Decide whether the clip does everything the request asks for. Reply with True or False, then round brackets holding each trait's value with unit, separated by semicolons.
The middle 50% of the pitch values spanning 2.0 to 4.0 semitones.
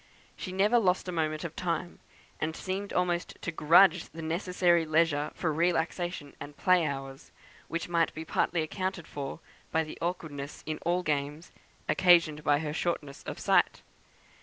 True (2.6 semitones)